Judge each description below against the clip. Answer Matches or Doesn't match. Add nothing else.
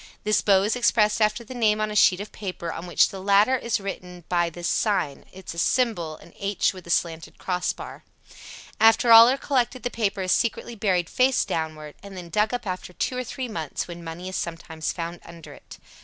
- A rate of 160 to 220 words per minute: Matches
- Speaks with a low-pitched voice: Doesn't match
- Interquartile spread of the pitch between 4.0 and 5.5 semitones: Matches